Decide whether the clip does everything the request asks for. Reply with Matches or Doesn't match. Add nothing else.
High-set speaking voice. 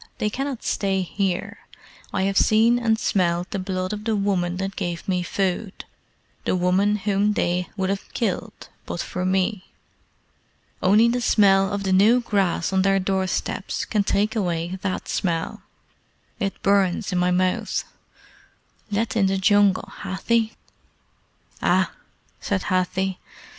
Matches